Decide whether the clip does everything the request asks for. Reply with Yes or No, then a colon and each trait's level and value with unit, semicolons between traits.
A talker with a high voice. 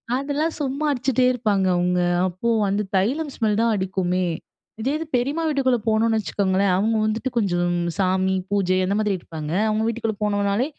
Yes: high, 215 Hz